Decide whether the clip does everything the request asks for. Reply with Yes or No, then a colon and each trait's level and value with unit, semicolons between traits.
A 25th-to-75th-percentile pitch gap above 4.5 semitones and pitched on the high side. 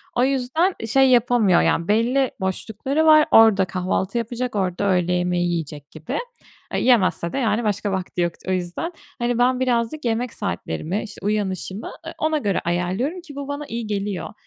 Yes: wide, 5.5 semitones; high, 215 Hz